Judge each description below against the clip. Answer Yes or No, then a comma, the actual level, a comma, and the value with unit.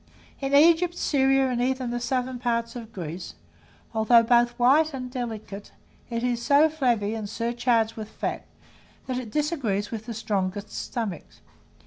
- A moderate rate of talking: Yes, average, 150 wpm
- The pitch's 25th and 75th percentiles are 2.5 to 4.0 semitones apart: Yes, average, 3.1 semitones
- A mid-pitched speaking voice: No, high, 240 Hz